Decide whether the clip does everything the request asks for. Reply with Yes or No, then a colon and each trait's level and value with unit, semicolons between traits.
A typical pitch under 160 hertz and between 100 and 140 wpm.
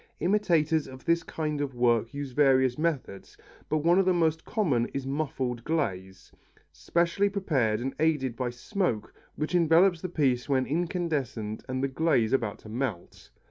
No: medium, 140 Hz; average, 160 wpm